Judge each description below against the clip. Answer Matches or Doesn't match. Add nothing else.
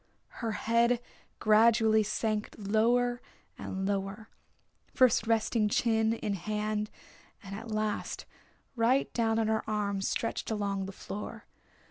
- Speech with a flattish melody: Matches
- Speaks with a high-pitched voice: Matches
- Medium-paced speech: Doesn't match